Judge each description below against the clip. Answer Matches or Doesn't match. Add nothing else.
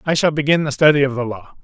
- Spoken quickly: Matches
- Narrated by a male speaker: Matches